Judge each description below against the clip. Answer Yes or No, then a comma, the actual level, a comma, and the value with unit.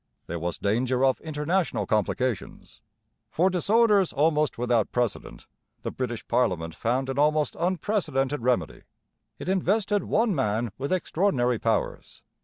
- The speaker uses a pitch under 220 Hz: Yes, low, 135 Hz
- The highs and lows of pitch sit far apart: Yes, wide, 7.0 semitones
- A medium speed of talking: No, slow, 125 wpm